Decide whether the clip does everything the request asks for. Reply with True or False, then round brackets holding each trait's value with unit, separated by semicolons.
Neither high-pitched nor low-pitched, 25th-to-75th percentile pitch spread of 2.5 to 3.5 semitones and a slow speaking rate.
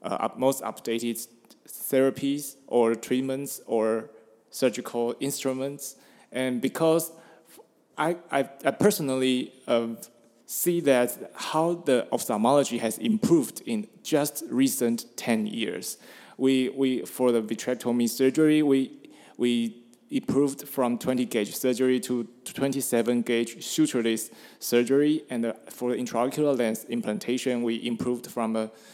False (125 Hz; 2.9 semitones; 120 wpm)